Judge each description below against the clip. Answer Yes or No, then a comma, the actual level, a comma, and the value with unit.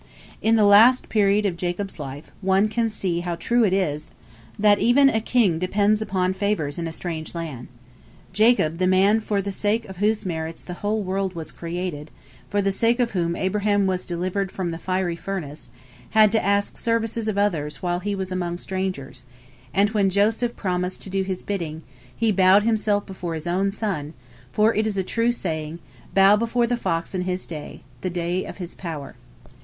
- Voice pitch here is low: No, high, 190 Hz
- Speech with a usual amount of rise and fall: Yes, average, 3.3 semitones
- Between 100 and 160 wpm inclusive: No, average, 190 wpm